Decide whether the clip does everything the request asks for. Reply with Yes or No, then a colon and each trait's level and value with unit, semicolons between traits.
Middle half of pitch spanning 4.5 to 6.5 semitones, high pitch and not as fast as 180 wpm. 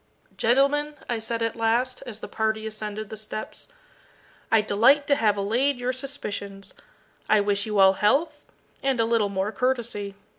No: average, 3.6 semitones; high, 225 Hz; average, 160 wpm